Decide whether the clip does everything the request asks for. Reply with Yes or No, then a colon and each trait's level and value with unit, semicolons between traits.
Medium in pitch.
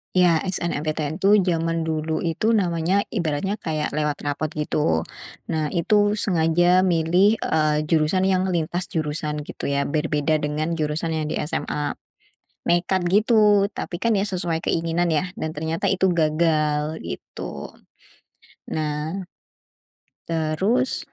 Yes: medium, 160 Hz